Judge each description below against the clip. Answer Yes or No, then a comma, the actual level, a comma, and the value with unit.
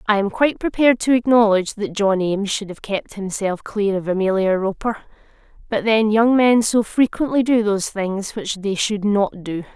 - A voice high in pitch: Yes, high, 210 Hz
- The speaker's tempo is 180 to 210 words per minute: Yes, average, 190 wpm